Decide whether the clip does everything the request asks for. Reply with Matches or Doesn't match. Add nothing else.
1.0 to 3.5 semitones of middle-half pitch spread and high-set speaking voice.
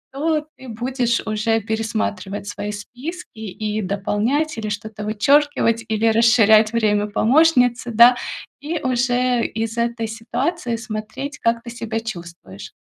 Matches